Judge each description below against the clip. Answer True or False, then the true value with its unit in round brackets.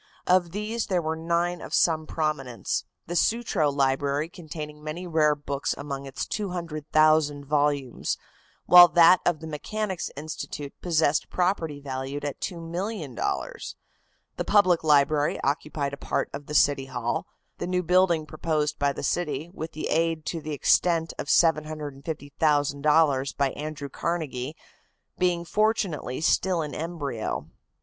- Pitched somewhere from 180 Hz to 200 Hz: False (155 Hz)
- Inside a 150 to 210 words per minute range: False (135 wpm)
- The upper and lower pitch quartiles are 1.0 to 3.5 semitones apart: True (3.1 semitones)